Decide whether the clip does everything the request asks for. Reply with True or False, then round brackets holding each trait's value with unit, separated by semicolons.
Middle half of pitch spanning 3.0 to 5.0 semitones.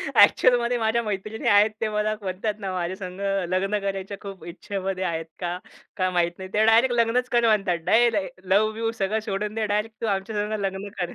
False (2.6 semitones)